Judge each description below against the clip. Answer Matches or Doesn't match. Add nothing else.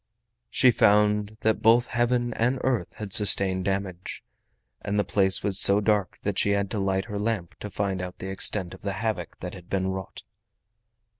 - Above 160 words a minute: Matches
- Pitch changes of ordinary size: Doesn't match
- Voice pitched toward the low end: Matches